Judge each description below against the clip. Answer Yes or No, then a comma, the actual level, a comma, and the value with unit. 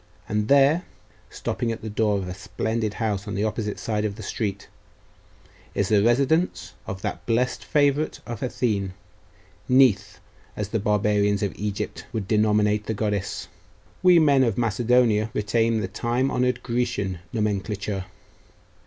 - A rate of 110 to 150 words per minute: Yes, average, 145 wpm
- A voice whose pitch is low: Yes, low, 110 Hz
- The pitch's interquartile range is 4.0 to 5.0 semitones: No, average, 2.9 semitones